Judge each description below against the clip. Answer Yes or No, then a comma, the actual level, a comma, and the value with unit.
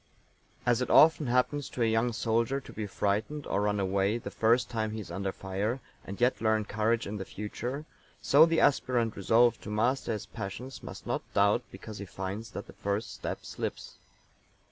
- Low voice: Yes, low, 110 Hz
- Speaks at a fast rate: No, average, 190 wpm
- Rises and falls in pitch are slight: No, average, 3.2 semitones